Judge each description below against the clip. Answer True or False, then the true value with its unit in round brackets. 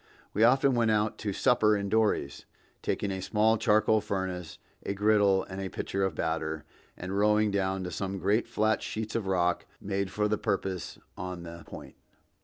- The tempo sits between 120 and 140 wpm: False (180 wpm)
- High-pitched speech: False (100 Hz)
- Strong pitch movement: False (2.4 semitones)